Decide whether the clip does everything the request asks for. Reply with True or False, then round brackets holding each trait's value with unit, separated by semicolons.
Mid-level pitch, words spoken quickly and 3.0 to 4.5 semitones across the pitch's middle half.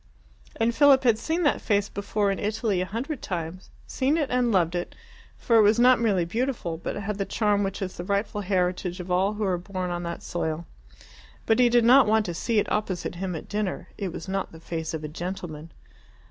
False (200 Hz; 220 wpm; 4.1 semitones)